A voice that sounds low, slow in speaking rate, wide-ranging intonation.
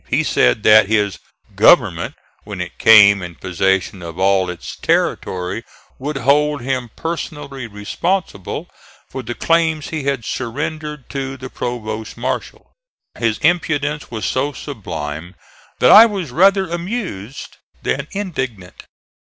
Yes: low, 130 Hz; slow, 130 wpm; wide, 6.9 semitones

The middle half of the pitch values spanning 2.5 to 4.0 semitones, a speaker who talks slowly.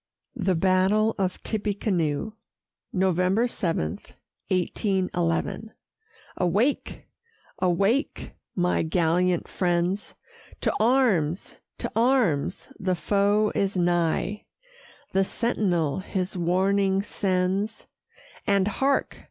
Yes: average, 2.9 semitones; slow, 85 wpm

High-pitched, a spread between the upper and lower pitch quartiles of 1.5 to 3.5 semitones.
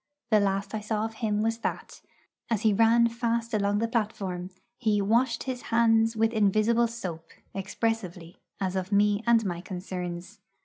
Yes: high, 215 Hz; average, 2.8 semitones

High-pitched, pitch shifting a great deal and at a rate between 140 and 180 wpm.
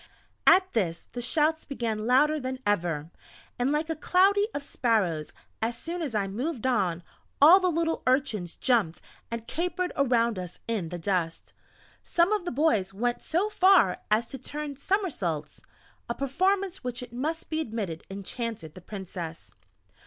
Yes: high, 245 Hz; wide, 8.3 semitones; average, 160 wpm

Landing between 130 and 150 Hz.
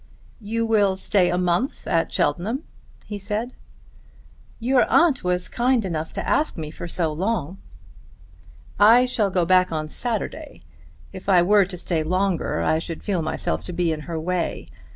No: medium, 185 Hz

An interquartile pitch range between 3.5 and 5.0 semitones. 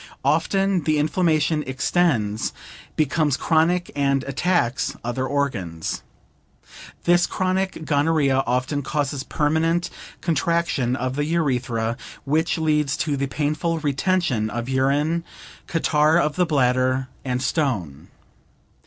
Yes: average, 4.0 semitones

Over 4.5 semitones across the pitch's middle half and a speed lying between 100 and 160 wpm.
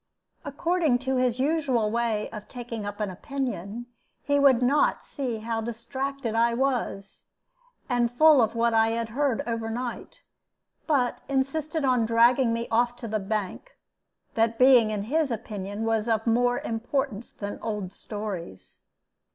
No: average, 3.1 semitones; average, 145 wpm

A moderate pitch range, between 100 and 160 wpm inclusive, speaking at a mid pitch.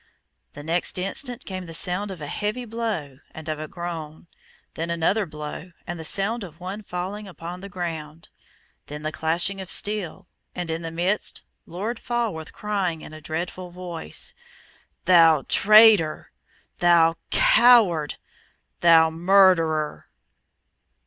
Yes: average, 3.6 semitones; slow, 135 wpm; medium, 175 Hz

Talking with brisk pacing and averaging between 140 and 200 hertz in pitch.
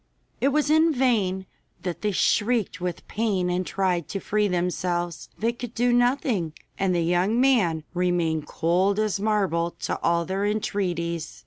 No: average, 155 wpm; high, 190 Hz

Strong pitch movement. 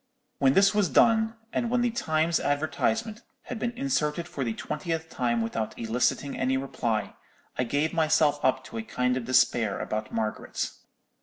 Yes: wide, 7.4 semitones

